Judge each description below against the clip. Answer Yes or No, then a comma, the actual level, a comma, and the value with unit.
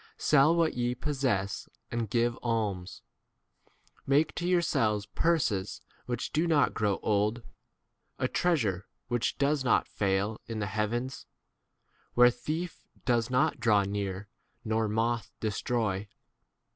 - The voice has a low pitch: Yes, low, 115 Hz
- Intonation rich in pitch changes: No, average, 4.4 semitones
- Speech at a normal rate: No, slow, 120 wpm